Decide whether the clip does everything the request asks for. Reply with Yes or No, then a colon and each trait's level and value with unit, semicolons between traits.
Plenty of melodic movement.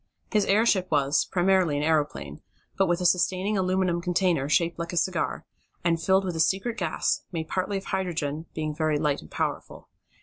No: average, 3.3 semitones